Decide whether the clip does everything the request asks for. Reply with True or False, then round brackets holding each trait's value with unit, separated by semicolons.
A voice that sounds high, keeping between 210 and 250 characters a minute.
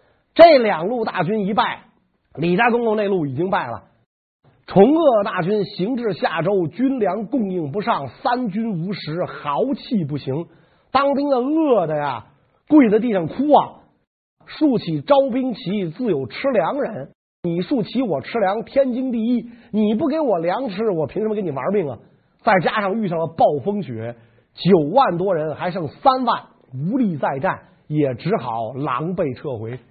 True (200 Hz; 230 characters per minute)